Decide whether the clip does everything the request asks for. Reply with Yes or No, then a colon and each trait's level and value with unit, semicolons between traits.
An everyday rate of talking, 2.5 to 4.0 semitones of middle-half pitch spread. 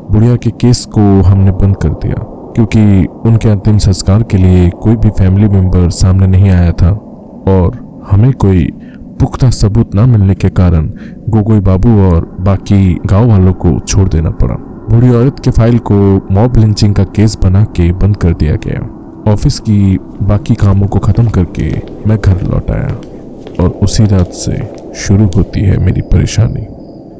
Yes: average, 170 wpm; average, 2.9 semitones